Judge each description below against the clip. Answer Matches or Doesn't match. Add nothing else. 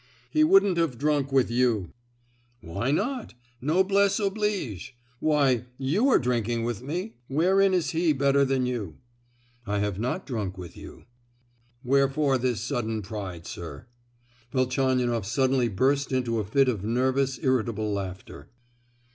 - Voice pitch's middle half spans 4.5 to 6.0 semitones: Matches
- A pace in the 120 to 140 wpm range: Matches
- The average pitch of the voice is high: Doesn't match